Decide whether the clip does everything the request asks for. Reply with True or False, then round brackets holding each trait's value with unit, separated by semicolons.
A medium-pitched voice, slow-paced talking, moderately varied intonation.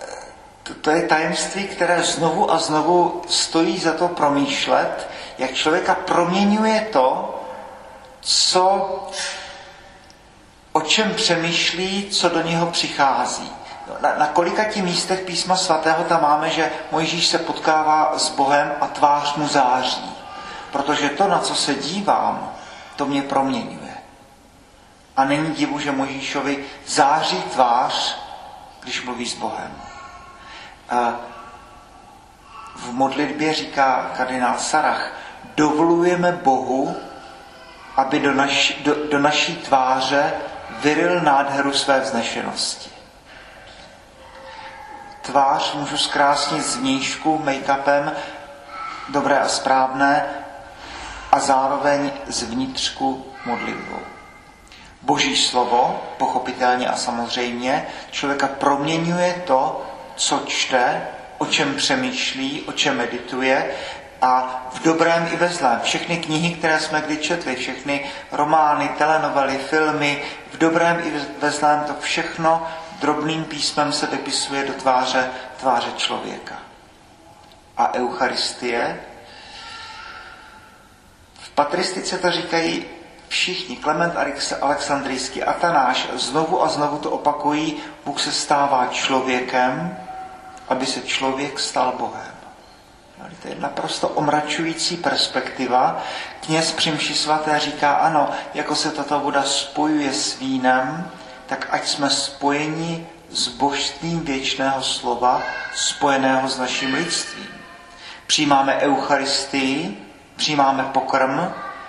True (150 Hz; 105 wpm; 3.7 semitones)